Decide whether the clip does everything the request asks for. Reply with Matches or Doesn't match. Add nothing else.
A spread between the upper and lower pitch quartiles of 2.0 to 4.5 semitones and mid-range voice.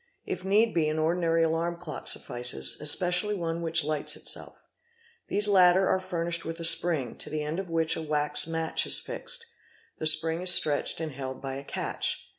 Matches